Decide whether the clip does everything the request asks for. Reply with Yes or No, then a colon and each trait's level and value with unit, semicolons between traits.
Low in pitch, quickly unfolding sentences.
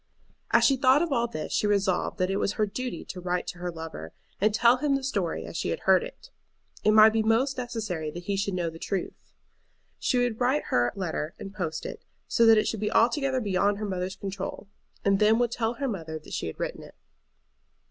No: high, 210 Hz; fast, 230 wpm